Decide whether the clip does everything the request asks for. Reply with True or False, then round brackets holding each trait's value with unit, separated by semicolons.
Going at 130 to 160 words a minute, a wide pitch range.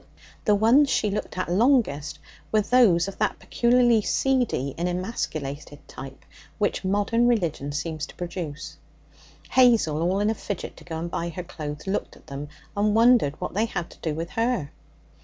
False (175 wpm; 6.4 semitones)